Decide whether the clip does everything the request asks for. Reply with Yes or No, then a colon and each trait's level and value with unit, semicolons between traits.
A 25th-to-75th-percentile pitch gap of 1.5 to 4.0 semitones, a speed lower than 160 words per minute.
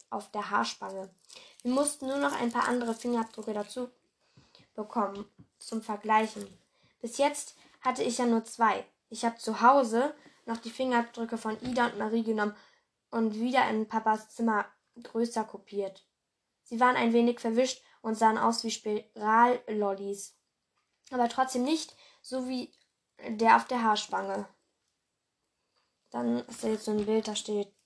Yes: narrow, 2.4 semitones; average, 150 wpm